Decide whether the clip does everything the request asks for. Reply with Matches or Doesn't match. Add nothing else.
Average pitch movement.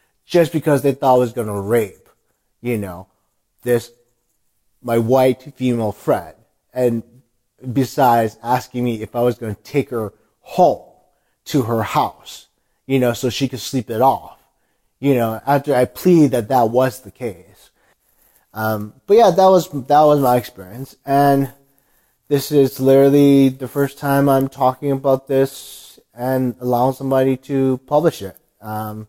Matches